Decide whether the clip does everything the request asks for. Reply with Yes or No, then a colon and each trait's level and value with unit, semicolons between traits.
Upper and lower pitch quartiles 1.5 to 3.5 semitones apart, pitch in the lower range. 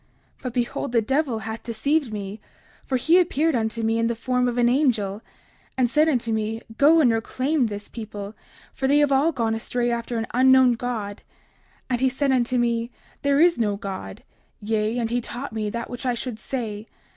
No: average, 2.9 semitones; high, 240 Hz